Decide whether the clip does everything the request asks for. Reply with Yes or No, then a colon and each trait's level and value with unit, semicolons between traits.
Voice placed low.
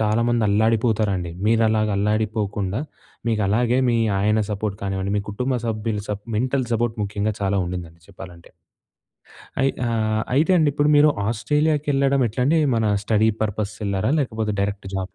Yes: low, 110 Hz